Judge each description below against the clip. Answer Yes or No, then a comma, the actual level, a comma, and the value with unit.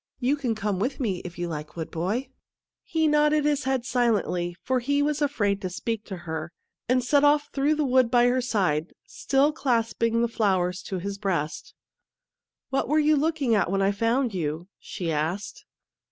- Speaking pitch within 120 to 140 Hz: No, high, 230 Hz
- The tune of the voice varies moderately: No, wide, 6.8 semitones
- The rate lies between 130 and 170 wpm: No, average, 195 wpm